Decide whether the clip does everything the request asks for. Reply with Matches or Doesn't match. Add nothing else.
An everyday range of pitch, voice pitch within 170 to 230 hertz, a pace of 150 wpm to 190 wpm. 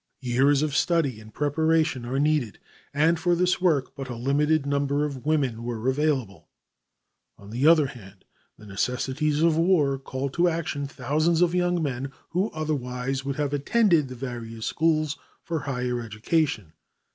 Doesn't match